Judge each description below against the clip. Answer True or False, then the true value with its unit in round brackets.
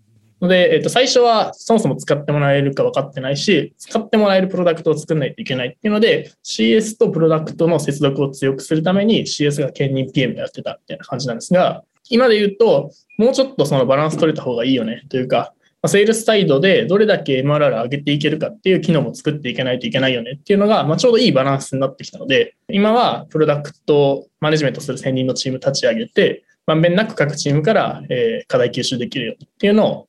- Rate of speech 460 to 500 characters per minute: True (495 characters per minute)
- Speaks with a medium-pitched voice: True (160 Hz)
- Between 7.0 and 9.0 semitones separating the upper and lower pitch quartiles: True (7.7 semitones)